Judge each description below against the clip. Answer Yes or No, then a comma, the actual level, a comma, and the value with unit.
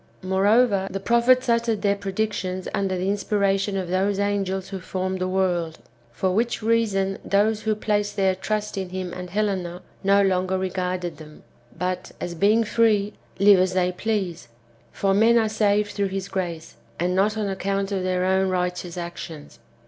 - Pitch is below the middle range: No, high, 195 Hz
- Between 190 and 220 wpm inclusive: No, average, 170 wpm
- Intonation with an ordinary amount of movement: No, narrow, 2.0 semitones